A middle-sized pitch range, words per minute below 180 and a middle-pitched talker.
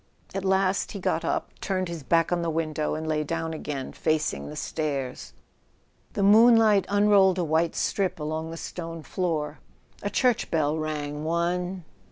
Yes: average, 3.6 semitones; average, 165 wpm; medium, 165 Hz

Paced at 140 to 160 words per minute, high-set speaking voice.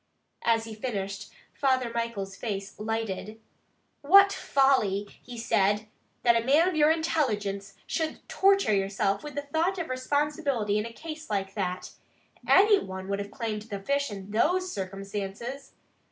Yes: average, 150 wpm; high, 225 Hz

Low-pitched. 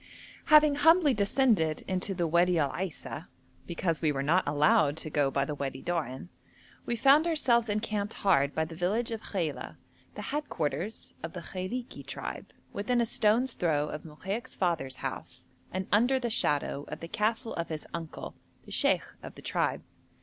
No: medium, 185 Hz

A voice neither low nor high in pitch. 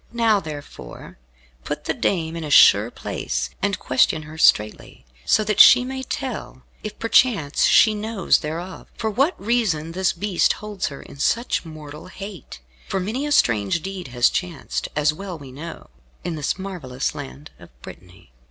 Yes: medium, 175 Hz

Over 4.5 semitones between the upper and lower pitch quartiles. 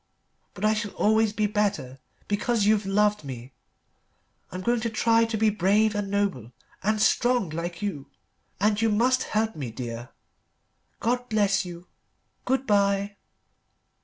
No: average, 2.9 semitones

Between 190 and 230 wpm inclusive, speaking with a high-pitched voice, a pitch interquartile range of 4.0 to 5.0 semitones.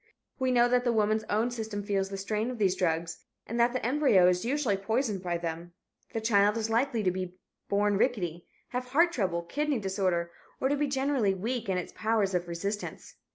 Yes: average, 200 wpm; high, 210 Hz; average, 4.7 semitones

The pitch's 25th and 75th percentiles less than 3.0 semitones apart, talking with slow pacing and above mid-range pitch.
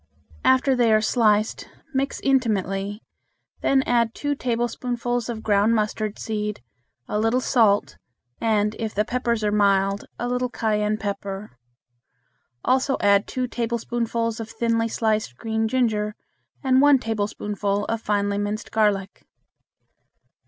Yes: narrow, 2.4 semitones; slow, 125 wpm; high, 220 Hz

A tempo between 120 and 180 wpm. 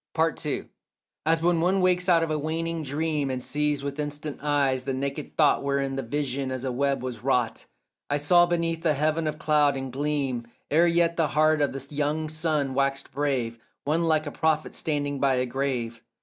No: average, 200 wpm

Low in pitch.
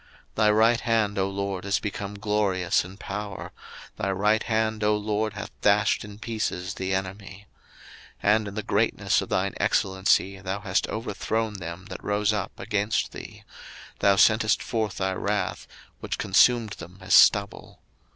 Yes: low, 105 Hz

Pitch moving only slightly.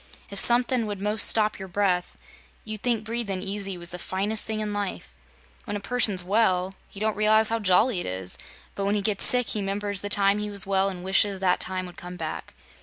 Yes: narrow, 2.3 semitones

